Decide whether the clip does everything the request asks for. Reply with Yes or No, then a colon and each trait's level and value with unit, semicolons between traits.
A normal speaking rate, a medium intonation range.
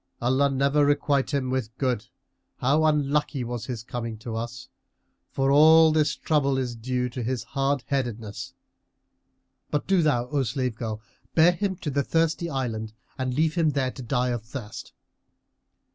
Yes: average, 160 wpm; average, 3.4 semitones